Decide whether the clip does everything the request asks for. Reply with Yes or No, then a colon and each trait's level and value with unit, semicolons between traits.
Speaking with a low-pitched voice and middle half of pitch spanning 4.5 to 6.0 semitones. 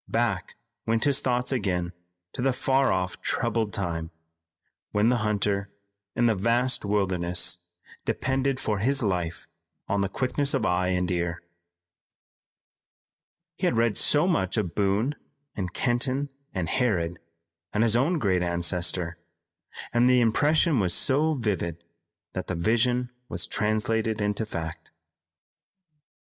Yes: low, 105 Hz; wide, 5.5 semitones